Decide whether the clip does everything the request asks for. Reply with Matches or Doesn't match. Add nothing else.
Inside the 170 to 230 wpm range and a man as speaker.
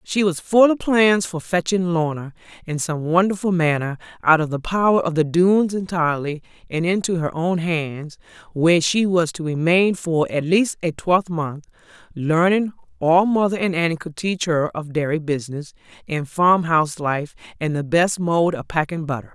Doesn't match